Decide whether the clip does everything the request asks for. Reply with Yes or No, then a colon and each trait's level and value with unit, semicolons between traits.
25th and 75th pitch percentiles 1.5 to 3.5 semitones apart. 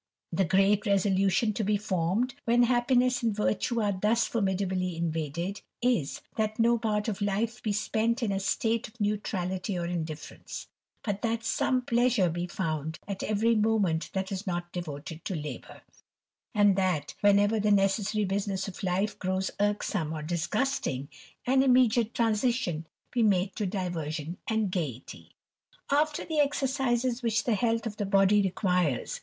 No: average, 4.0 semitones